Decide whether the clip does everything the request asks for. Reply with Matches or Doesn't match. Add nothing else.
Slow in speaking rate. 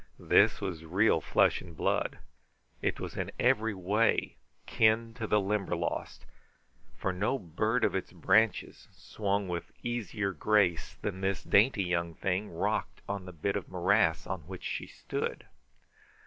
Doesn't match